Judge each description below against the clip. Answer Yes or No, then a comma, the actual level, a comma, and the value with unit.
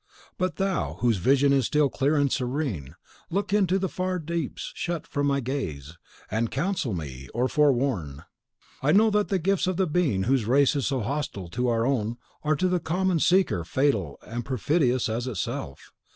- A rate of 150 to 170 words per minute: No, average, 180 wpm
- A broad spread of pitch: Yes, wide, 6.9 semitones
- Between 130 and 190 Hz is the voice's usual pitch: Yes, medium, 140 Hz